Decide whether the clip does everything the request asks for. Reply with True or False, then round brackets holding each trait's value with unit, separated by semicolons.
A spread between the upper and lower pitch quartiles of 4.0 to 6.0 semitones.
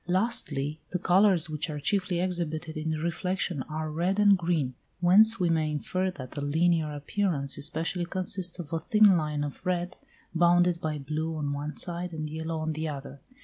False (2.9 semitones)